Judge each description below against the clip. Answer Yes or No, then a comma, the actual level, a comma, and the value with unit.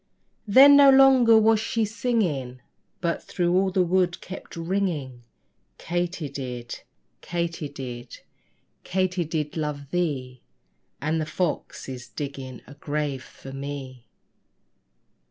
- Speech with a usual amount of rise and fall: No, wide, 5.7 semitones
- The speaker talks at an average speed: No, slow, 120 wpm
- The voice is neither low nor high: Yes, medium, 160 Hz